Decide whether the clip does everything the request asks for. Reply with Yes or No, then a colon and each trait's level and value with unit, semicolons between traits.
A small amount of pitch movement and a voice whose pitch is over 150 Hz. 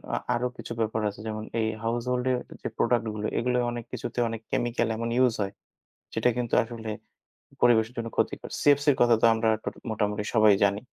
No: narrow, 1.9 semitones; low, 115 Hz